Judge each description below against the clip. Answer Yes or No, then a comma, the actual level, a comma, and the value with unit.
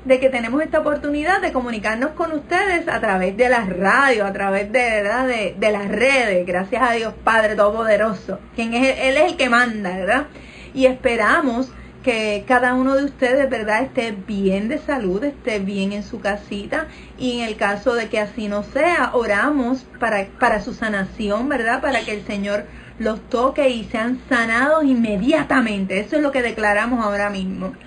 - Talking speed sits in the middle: Yes, average, 180 wpm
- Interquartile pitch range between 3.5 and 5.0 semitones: Yes, average, 4.2 semitones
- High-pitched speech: Yes, high, 235 Hz